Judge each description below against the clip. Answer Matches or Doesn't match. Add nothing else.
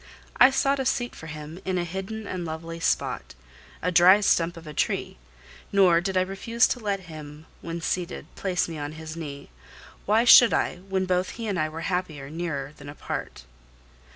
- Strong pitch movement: Doesn't match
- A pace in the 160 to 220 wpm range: Matches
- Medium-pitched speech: Matches